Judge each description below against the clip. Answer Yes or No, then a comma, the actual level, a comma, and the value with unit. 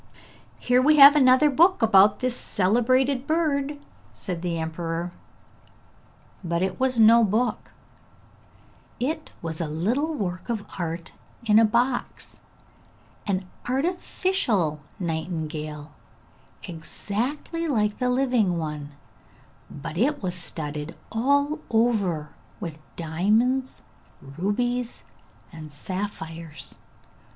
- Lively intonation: Yes, wide, 7.5 semitones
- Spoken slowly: Yes, slow, 105 wpm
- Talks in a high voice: Yes, high, 210 Hz